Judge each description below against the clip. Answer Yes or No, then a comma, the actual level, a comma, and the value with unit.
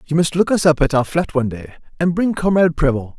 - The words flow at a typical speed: No, fast, 265 wpm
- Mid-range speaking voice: Yes, medium, 155 Hz